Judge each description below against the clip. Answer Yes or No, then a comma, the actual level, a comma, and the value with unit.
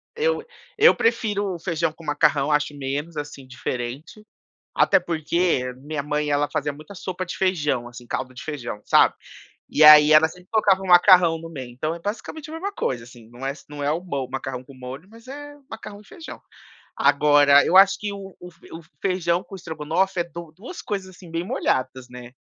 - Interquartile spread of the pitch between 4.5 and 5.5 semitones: Yes, average, 5.1 semitones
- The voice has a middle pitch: Yes, medium, 160 Hz